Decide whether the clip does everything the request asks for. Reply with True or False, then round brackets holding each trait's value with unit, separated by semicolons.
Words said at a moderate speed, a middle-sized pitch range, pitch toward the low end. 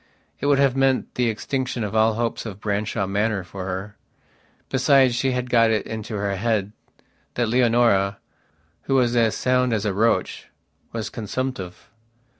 True (160 wpm; 3.4 semitones; 115 Hz)